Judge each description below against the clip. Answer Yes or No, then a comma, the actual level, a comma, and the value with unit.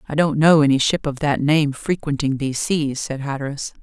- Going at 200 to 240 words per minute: Yes, fast, 205 wpm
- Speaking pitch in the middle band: Yes, medium, 145 Hz